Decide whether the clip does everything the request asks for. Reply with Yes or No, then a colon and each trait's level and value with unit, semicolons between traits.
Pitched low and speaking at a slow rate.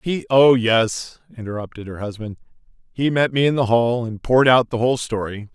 No: low, 120 Hz; average, 185 wpm